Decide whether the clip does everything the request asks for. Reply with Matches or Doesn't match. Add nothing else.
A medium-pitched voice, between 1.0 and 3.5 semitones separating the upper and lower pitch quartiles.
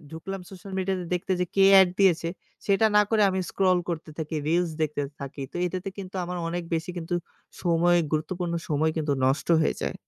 Matches